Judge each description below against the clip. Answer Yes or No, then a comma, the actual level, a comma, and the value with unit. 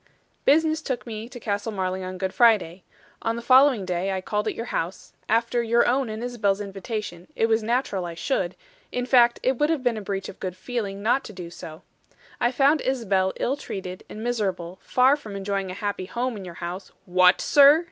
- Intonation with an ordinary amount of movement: Yes, average, 4.5 semitones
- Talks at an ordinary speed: No, fast, 210 wpm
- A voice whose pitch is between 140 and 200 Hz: No, high, 215 Hz